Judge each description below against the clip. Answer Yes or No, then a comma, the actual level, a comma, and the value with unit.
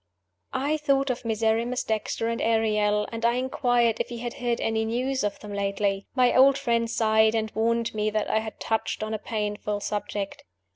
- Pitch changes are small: Yes, narrow, 2.1 semitones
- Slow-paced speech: No, average, 190 wpm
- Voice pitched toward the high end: Yes, high, 225 Hz